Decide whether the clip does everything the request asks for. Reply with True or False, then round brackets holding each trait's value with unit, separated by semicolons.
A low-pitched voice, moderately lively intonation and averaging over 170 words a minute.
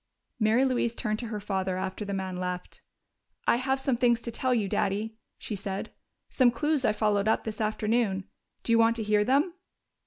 False (220 Hz; 3.1 semitones; 195 wpm)